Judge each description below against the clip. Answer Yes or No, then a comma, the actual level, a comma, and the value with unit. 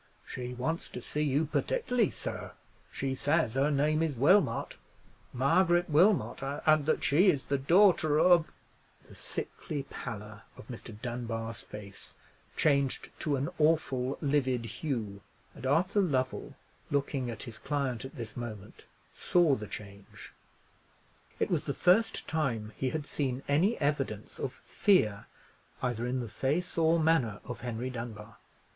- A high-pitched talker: No, low, 135 Hz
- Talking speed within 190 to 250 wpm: No, average, 140 wpm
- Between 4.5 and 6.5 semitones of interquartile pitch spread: Yes, average, 4.9 semitones